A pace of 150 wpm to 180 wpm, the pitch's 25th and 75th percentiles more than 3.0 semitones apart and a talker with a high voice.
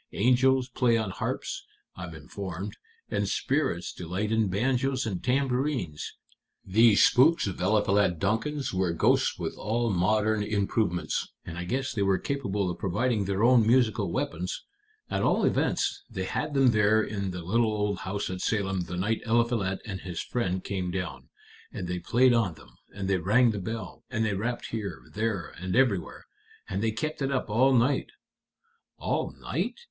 No: average, 170 wpm; average, 4.3 semitones; low, 105 Hz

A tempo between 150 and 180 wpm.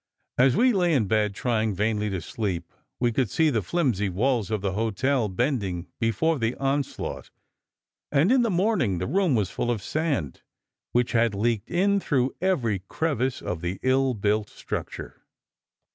Yes: average, 165 wpm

